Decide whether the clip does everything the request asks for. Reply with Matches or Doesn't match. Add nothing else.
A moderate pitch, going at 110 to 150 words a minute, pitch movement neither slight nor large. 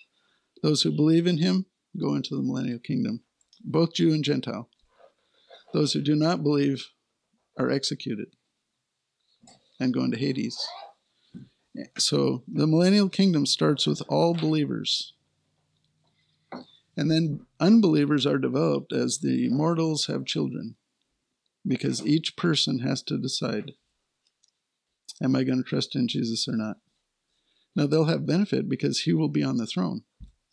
Matches